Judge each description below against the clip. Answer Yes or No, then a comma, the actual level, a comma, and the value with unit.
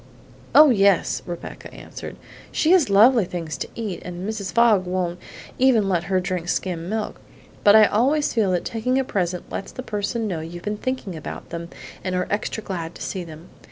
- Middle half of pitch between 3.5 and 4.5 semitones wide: Yes, average, 4.1 semitones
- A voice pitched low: No, high, 195 Hz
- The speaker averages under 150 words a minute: No, average, 190 wpm